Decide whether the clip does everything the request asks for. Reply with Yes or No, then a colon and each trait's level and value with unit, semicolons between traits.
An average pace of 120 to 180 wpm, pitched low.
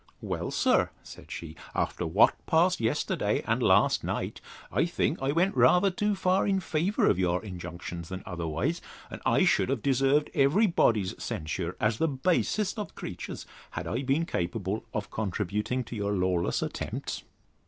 Yes: average, 165 wpm; low, 120 Hz